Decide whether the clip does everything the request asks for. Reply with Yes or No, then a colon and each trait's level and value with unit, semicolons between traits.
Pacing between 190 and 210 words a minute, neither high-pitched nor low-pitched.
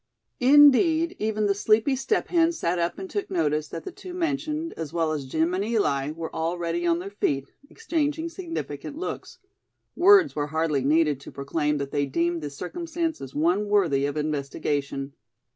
No: average, 175 wpm; medium, 175 Hz